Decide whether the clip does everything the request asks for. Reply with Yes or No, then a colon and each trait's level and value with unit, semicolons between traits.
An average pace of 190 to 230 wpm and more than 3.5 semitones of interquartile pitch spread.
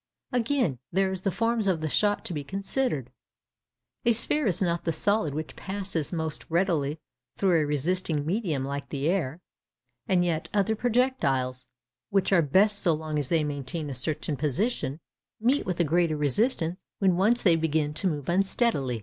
No: average, 175 wpm; average, 5.1 semitones